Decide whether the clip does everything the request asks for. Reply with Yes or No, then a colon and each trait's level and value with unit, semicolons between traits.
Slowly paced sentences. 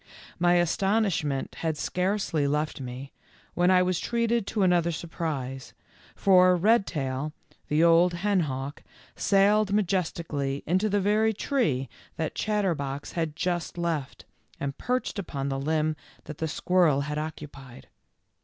Yes: slow, 125 wpm